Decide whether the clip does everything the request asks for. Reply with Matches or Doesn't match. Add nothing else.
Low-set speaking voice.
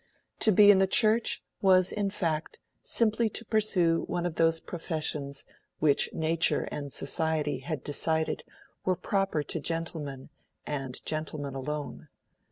Doesn't match